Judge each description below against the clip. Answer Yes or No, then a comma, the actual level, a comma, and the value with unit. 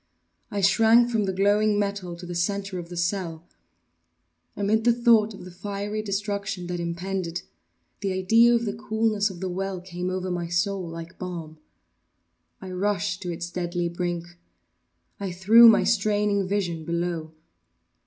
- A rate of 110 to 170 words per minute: Yes, average, 155 wpm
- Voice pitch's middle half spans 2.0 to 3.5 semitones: Yes, average, 2.9 semitones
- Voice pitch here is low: No, high, 190 Hz